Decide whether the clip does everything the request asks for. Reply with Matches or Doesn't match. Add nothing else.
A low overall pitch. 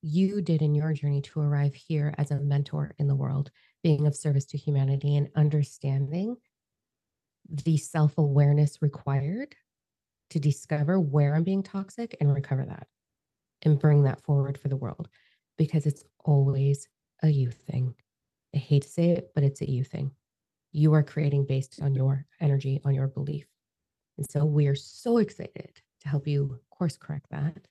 Doesn't match